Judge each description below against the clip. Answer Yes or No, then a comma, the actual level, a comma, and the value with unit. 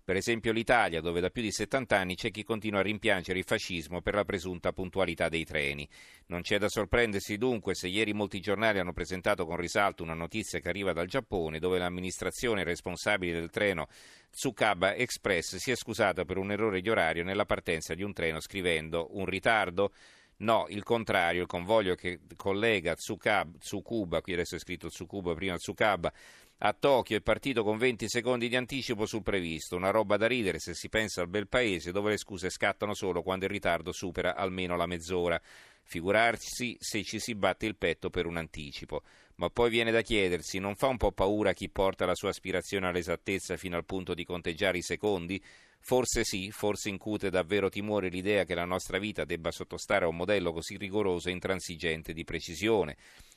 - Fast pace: Yes, fast, 190 wpm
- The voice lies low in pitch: Yes, very low, 95 Hz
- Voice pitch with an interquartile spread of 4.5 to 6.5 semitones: No, average, 3.1 semitones